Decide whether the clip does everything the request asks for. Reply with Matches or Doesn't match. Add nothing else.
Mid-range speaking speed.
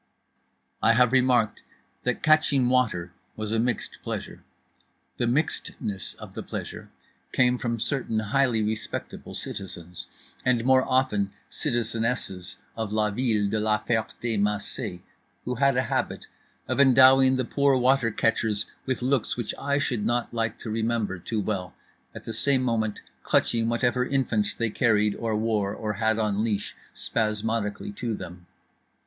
Matches